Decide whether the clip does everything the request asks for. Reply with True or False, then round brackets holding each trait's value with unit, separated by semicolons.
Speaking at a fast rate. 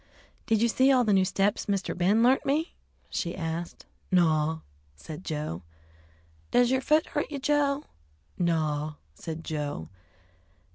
False (140 wpm)